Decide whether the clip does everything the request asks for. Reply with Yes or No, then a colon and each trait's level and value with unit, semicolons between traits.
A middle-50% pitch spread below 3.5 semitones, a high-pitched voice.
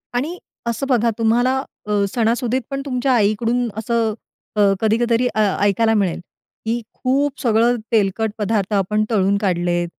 Yes: average, 2.7 semitones; high, 225 Hz